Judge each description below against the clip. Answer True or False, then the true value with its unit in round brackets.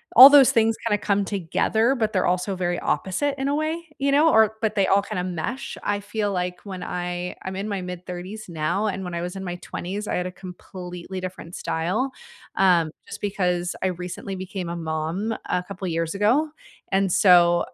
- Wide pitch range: False (3.1 semitones)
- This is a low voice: False (190 Hz)